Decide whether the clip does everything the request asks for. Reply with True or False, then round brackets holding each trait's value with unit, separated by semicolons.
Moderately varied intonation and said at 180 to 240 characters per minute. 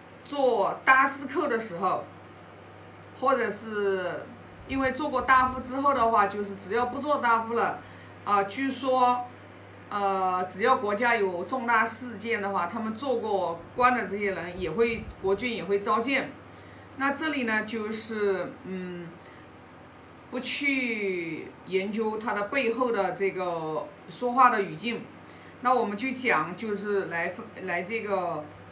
True (5.0 semitones; 200 characters per minute)